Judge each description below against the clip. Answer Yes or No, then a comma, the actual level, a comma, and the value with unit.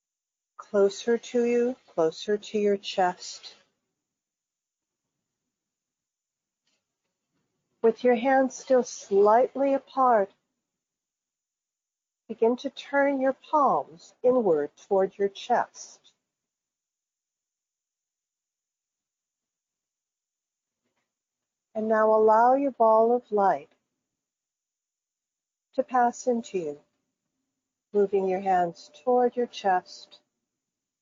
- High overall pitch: Yes, high, 225 Hz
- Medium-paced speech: No, slow, 75 wpm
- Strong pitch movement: No, average, 4.3 semitones